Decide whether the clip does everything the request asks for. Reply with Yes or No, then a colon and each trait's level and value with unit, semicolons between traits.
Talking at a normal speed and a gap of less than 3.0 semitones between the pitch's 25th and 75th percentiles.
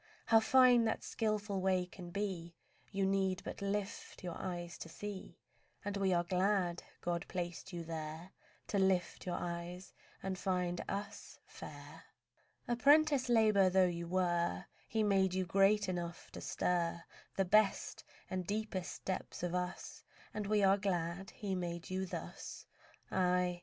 Yes: average, 150 wpm; narrow, 2.4 semitones